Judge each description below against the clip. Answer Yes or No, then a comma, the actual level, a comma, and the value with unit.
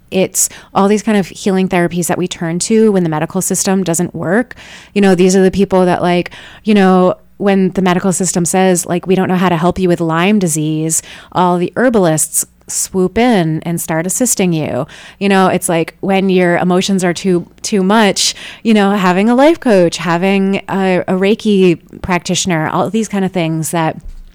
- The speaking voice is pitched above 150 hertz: Yes, medium, 185 Hz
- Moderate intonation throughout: No, narrow, 2.2 semitones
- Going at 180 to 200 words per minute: Yes, average, 195 wpm